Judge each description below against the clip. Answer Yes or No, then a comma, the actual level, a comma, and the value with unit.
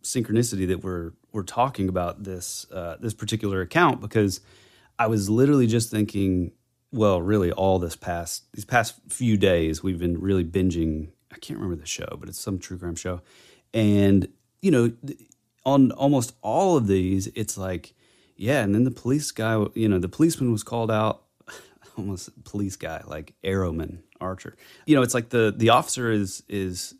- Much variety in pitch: No, average, 3.9 semitones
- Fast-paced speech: No, average, 175 wpm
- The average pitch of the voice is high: No, low, 105 Hz